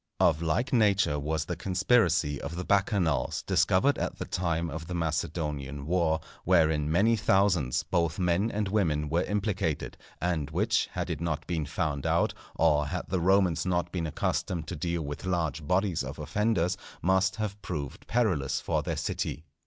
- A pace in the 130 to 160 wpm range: No, average, 170 wpm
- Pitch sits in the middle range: No, very low, 85 Hz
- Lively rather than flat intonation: No, average, 3.5 semitones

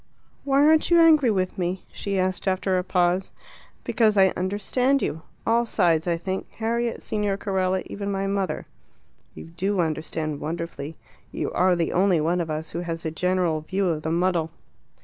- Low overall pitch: No, medium, 185 Hz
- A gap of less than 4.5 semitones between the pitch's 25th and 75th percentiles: Yes, average, 3.2 semitones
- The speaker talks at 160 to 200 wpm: Yes, average, 175 wpm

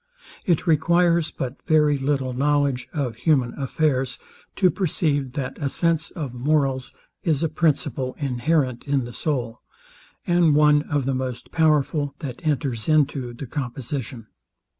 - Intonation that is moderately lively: Yes, average, 3.3 semitones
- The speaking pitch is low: No, medium, 145 Hz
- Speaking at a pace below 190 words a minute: Yes, average, 140 wpm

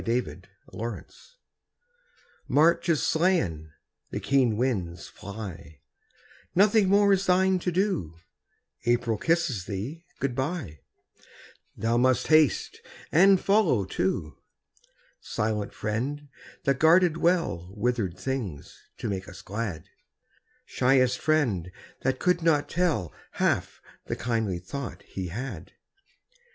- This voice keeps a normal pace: No, slow, 120 wpm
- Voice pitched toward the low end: Yes, low, 125 Hz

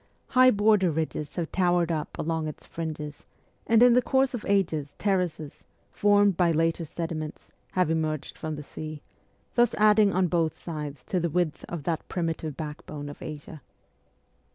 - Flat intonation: No, average, 3.9 semitones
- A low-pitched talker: No, medium, 165 Hz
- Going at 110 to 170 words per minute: Yes, average, 165 wpm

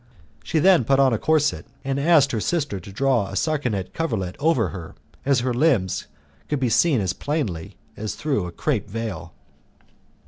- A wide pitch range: Yes, wide, 6.7 semitones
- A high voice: No, low, 130 Hz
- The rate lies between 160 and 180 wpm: Yes, average, 175 wpm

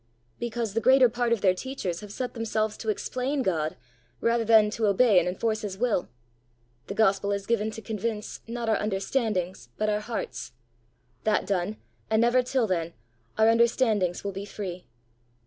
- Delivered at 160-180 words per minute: Yes, average, 170 wpm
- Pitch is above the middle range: Yes, high, 215 Hz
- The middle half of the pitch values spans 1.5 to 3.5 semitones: Yes, average, 3.0 semitones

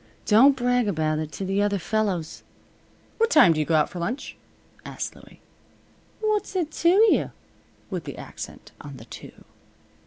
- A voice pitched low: No, high, 205 Hz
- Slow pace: No, average, 165 wpm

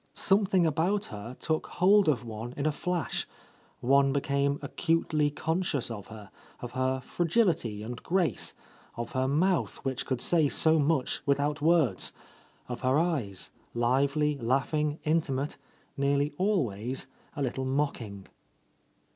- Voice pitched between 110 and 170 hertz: Yes, medium, 140 Hz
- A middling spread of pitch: Yes, average, 4.3 semitones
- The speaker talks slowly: Yes, slow, 130 wpm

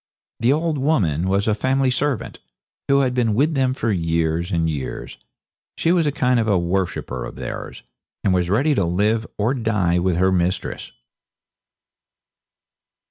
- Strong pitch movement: Yes, wide, 6.8 semitones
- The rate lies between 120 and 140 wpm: No, average, 155 wpm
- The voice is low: Yes, low, 105 Hz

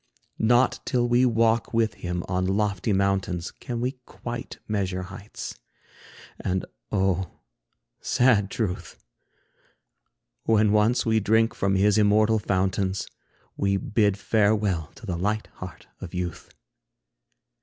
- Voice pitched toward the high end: No, low, 100 Hz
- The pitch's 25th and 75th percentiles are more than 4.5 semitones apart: No, average, 2.8 semitones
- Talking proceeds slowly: Yes, slow, 120 wpm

